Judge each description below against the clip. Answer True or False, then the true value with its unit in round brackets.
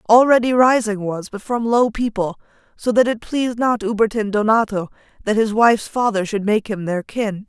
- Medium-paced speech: True (185 wpm)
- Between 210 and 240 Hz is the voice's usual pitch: True (220 Hz)